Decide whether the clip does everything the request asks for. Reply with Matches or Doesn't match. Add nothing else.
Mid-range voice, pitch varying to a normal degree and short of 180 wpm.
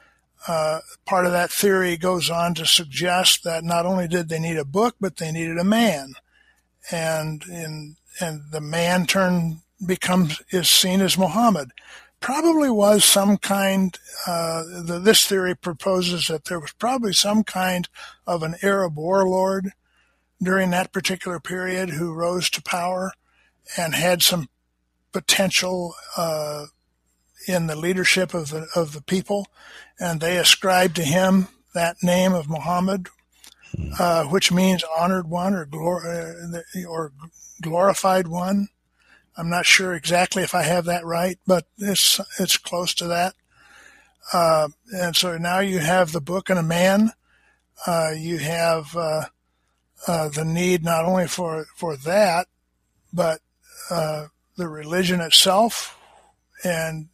Doesn't match